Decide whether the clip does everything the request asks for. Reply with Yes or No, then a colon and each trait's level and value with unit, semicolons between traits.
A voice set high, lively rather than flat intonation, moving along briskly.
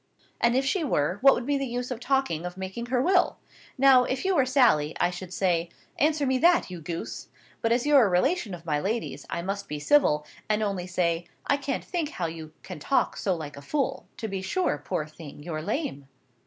Yes: high, 205 Hz; wide, 8.2 semitones; fast, 220 wpm